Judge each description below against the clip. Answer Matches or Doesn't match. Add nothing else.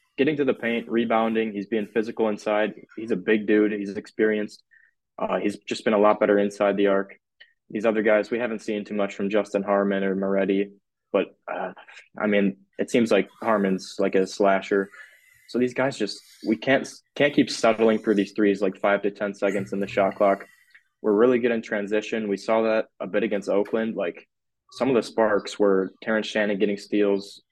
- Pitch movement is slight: Matches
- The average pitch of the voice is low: Matches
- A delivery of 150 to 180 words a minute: Doesn't match